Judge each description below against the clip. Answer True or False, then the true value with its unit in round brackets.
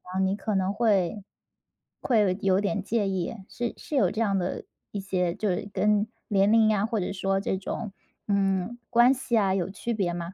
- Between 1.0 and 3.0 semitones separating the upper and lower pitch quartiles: True (2.4 semitones)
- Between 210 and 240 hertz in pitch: False (200 Hz)